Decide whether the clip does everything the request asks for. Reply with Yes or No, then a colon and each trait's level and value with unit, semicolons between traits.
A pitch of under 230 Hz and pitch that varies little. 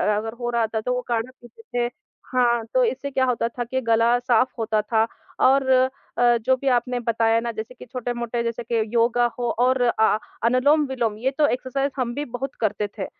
No: high, 240 Hz; narrow, 2.0 semitones